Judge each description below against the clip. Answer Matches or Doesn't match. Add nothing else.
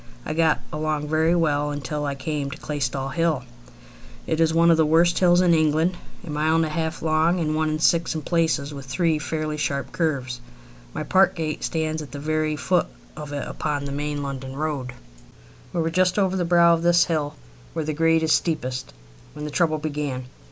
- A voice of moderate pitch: Matches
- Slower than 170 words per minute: Doesn't match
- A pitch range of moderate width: Doesn't match